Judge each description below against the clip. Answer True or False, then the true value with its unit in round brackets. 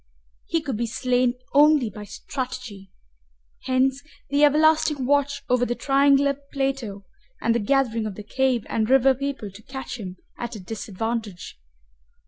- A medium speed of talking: True (145 wpm)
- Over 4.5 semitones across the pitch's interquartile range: False (3.9 semitones)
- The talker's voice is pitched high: True (255 Hz)